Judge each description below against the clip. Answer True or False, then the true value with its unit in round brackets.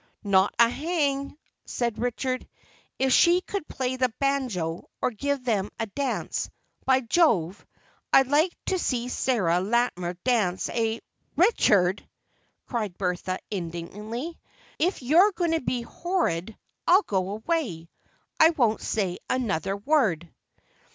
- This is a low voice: False (240 Hz)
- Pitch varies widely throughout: True (6.6 semitones)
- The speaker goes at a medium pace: False (125 wpm)